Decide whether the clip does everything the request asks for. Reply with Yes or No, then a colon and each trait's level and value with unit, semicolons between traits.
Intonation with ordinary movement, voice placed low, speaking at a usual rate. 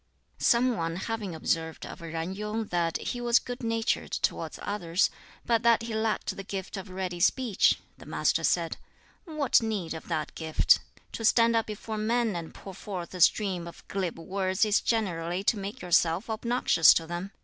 No: average, 4.6 semitones; high, 195 Hz; average, 180 wpm